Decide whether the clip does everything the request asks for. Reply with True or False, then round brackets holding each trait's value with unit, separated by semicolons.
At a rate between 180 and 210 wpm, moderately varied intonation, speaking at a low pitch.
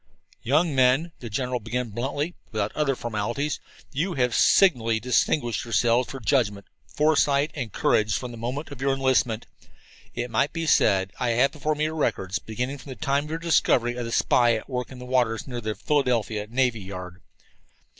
True (185 wpm; 3.8 semitones; 125 Hz)